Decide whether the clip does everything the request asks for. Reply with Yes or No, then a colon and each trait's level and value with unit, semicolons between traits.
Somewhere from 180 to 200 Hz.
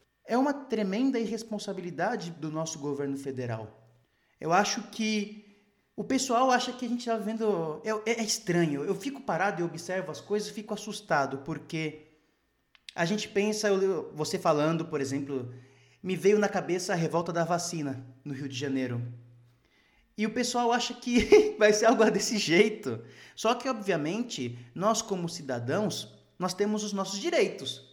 Yes: high, 190 Hz